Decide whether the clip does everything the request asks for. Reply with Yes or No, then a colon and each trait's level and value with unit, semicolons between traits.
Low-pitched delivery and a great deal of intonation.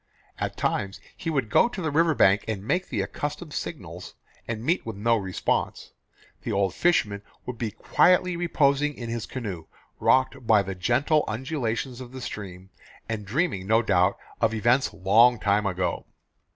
Yes: low, 115 Hz; wide, 5.9 semitones